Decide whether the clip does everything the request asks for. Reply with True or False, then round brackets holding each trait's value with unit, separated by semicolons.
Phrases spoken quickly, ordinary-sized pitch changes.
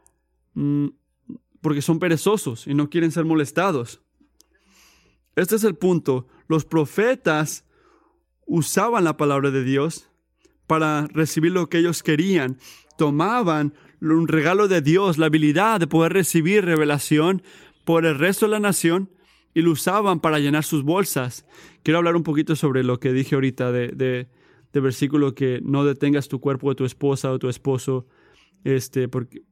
False (150 wpm; 3.7 semitones)